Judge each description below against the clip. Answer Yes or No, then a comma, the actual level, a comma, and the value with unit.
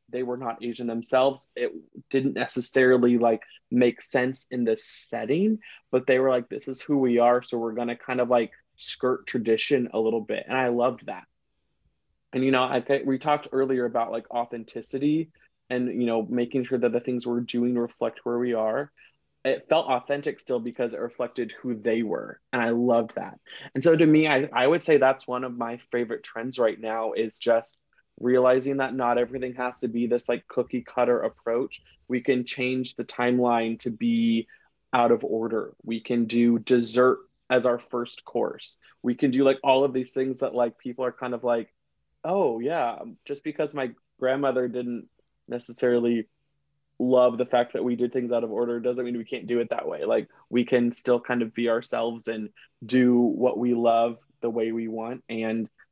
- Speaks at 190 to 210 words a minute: Yes, average, 200 wpm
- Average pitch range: No, narrow, 1.6 semitones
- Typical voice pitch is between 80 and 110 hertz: No, low, 125 Hz